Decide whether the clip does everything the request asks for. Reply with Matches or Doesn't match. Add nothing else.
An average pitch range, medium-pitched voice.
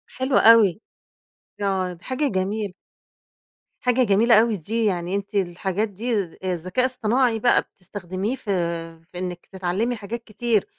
Doesn't match